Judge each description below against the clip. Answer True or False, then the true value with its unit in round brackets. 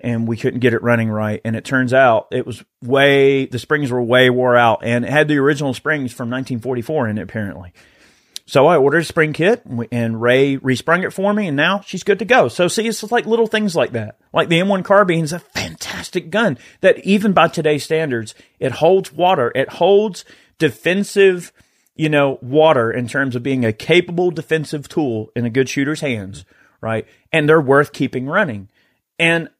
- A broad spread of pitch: True (5.7 semitones)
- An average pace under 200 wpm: False (205 wpm)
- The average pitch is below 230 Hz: True (140 Hz)